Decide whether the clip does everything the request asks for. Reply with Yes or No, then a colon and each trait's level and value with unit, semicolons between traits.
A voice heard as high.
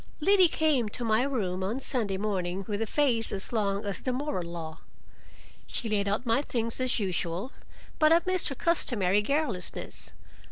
Yes: high, 225 Hz